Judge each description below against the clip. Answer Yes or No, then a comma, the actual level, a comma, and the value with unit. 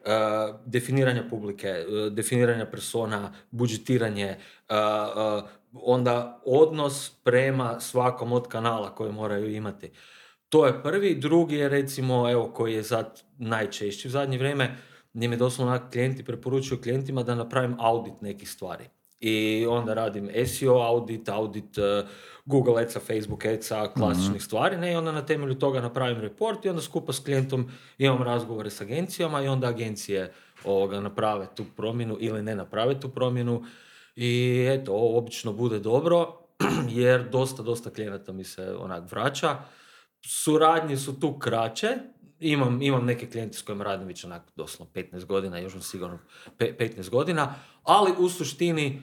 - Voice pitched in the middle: No, low, 120 Hz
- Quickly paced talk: No, average, 145 wpm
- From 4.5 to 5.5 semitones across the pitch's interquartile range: No, average, 3.6 semitones